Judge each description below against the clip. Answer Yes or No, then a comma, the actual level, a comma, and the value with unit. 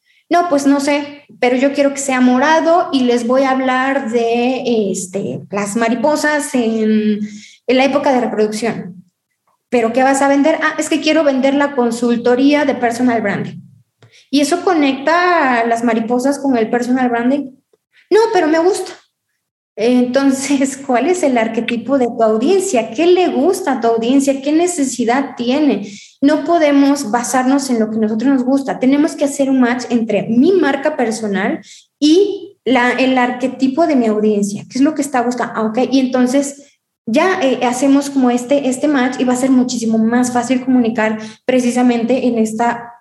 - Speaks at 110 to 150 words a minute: No, average, 175 wpm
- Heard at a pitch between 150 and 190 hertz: No, very high, 255 Hz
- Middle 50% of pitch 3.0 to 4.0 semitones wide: Yes, average, 3.3 semitones